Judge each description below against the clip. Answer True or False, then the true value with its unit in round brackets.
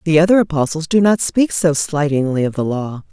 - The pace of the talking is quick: True (210 wpm)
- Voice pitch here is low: False (160 Hz)